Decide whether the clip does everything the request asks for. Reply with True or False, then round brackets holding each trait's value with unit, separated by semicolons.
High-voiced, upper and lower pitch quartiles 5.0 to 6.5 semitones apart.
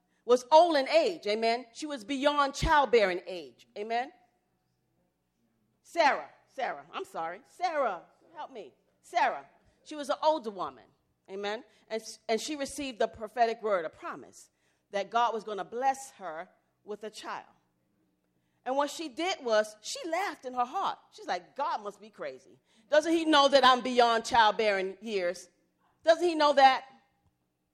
True (235 Hz; 5.6 semitones)